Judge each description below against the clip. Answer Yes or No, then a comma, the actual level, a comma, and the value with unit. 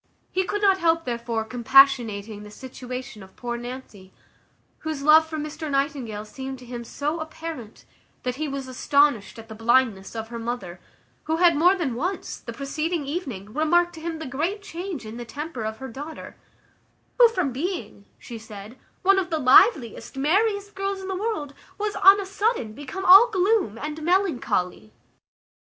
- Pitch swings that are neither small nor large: No, wide, 6.8 semitones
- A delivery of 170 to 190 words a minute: Yes, average, 175 wpm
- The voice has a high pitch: Yes, very high, 285 Hz